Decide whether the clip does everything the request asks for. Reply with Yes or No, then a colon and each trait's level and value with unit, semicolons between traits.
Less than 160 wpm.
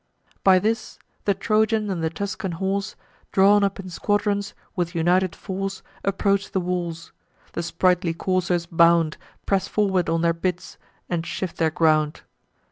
Yes: average, 145 wpm